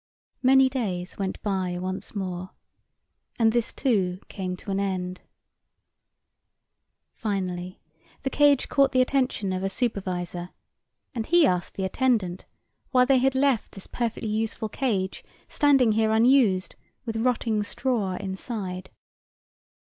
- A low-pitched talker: No, high, 210 Hz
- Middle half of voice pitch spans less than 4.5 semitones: No, average, 5.2 semitones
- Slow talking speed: Yes, slow, 125 wpm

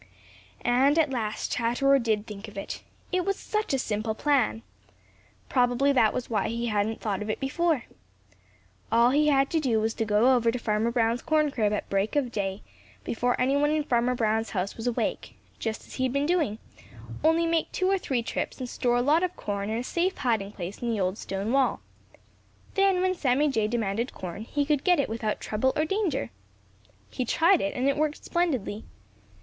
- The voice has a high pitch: Yes, high, 245 Hz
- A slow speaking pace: No, fast, 205 wpm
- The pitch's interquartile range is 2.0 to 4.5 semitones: No, average, 5.2 semitones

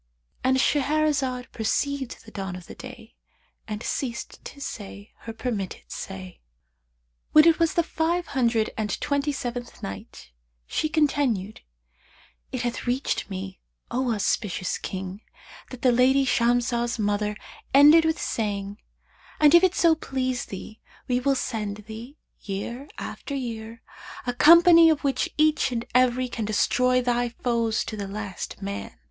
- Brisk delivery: No, average, 140 wpm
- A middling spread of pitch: Yes, average, 4.7 semitones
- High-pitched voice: Yes, high, 245 Hz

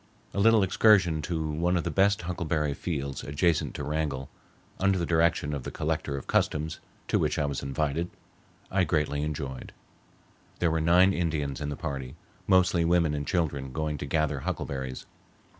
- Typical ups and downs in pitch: Yes, average, 3.4 semitones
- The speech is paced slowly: No, average, 170 wpm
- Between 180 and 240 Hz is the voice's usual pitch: No, very low, 80 Hz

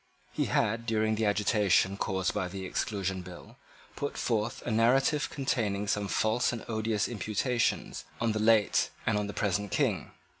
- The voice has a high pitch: No, low, 110 Hz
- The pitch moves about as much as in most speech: No, narrow, 2.3 semitones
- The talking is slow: No, average, 160 wpm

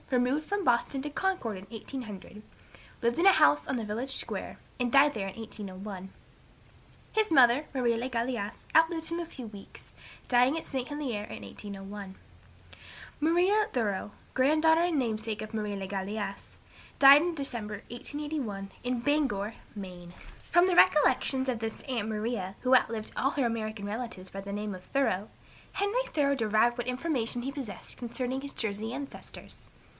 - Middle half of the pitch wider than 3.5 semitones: Yes, average, 5.1 semitones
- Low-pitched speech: No, high, 240 Hz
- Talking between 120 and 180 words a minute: Yes, average, 160 wpm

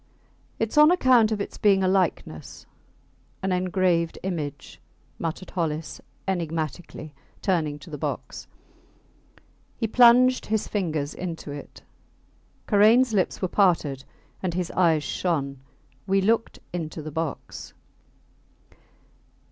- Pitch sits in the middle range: Yes, medium, 180 Hz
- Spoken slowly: Yes, slow, 115 wpm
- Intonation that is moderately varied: Yes, average, 4.7 semitones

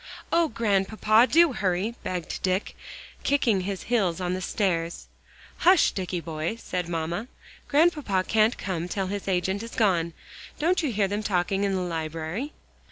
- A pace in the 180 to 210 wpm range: No, average, 155 wpm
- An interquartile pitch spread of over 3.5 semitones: Yes, average, 4.2 semitones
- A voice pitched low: No, high, 195 Hz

